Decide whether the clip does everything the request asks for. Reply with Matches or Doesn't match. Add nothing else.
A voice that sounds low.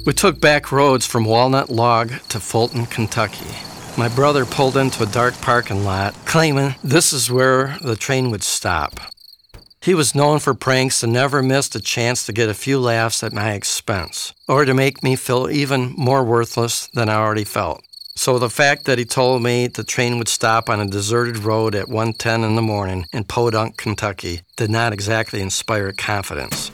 Matches